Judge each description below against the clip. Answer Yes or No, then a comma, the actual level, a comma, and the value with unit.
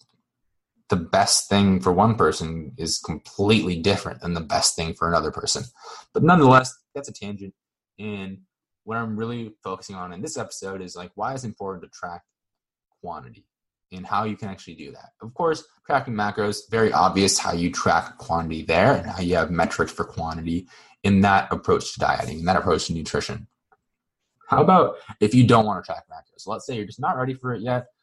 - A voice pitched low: Yes, low, 100 Hz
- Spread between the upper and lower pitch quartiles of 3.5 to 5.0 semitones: Yes, average, 4.1 semitones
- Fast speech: No, average, 195 wpm